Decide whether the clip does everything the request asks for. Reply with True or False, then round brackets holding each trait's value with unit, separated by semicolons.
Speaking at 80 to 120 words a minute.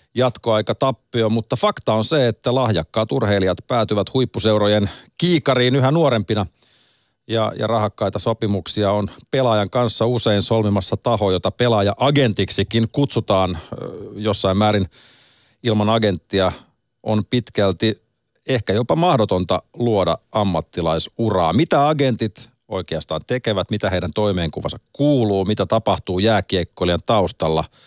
True (110 wpm)